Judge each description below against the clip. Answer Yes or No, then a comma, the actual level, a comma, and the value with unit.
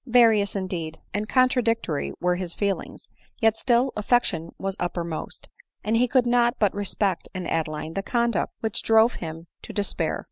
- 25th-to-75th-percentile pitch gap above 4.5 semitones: Yes, average, 5.0 semitones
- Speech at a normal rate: Yes, average, 165 wpm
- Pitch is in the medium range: No, high, 205 Hz